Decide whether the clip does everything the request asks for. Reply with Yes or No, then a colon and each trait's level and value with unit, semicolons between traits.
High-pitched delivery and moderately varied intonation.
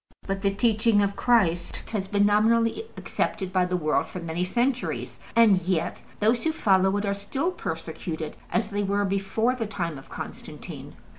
Yes: high, 200 Hz; average, 3.7 semitones